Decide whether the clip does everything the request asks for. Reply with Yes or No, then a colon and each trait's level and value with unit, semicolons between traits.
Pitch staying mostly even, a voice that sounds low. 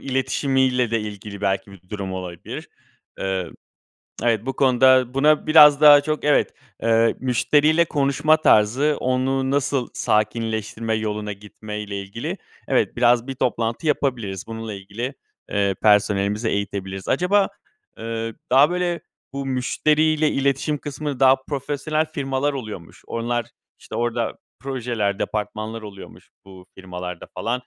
No: average, 4.8 semitones; low, 120 Hz